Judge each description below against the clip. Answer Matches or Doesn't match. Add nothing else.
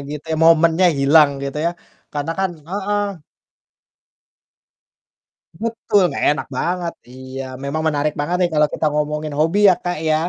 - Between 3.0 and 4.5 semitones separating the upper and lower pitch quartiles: Matches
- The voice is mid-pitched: Matches